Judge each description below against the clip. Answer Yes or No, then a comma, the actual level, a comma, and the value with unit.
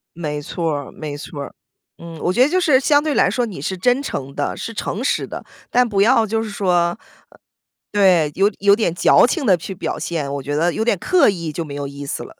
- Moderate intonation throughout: No, wide, 6.9 semitones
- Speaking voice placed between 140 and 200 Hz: Yes, medium, 185 Hz